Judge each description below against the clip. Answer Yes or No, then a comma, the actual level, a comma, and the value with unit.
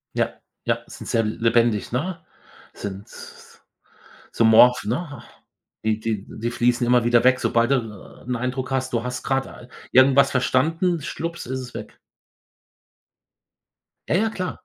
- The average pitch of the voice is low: Yes, low, 125 Hz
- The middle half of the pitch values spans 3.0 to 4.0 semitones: No, narrow, 2.5 semitones